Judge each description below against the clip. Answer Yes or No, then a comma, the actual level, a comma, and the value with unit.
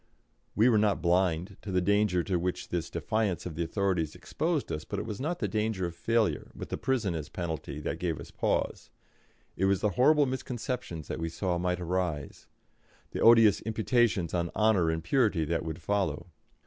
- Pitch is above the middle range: No, very low, 95 Hz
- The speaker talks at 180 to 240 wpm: Yes, average, 190 wpm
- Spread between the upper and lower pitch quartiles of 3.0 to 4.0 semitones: No, average, 4.5 semitones